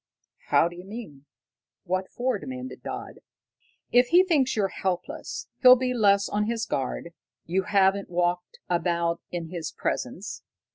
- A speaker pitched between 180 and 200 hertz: Yes, high, 190 Hz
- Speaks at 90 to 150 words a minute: Yes, average, 140 wpm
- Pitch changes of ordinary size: No, wide, 5.7 semitones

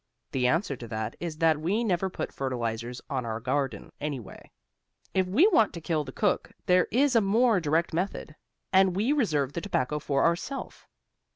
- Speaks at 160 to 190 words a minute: Yes, average, 180 wpm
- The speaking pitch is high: No, medium, 165 Hz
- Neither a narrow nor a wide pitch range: No, wide, 6.3 semitones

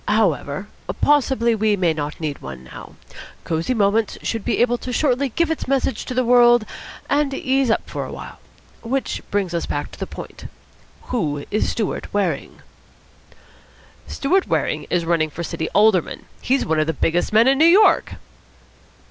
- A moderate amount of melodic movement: No, wide, 7.4 semitones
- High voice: Yes, high, 220 Hz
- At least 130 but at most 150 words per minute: No, average, 170 wpm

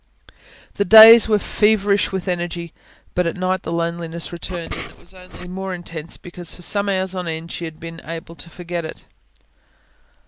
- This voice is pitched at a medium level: Yes, medium, 175 Hz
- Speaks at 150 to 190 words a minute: Yes, average, 180 wpm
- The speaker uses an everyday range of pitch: No, narrow, 2.2 semitones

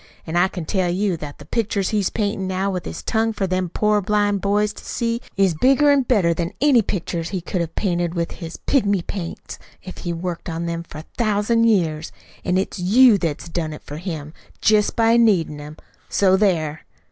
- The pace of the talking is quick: Yes, fast, 210 wpm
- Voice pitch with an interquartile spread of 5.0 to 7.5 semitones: No, average, 3.8 semitones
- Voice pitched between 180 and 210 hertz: Yes, medium, 185 Hz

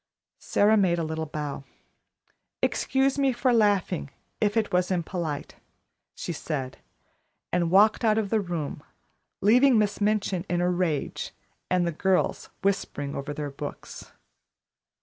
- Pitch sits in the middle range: Yes, medium, 180 Hz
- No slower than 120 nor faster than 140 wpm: Yes, slow, 135 wpm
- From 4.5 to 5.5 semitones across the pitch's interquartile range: Yes, average, 5.1 semitones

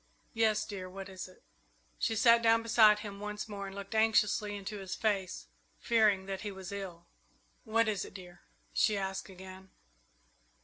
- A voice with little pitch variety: Yes, narrow, 2.3 semitones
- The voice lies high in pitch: Yes, high, 200 Hz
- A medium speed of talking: Yes, average, 170 wpm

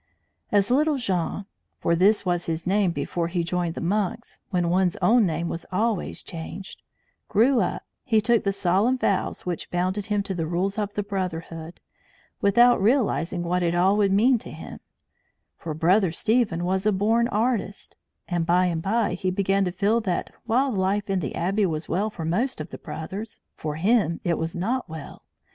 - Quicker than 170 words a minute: Yes, average, 185 wpm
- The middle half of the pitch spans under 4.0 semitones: Yes, average, 3.6 semitones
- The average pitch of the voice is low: No, high, 190 Hz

